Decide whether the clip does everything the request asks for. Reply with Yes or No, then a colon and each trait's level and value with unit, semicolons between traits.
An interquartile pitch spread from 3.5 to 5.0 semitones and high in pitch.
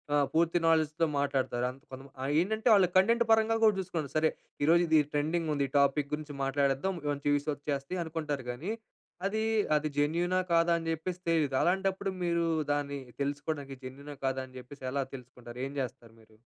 No: average, 3.8 semitones; medium, 150 Hz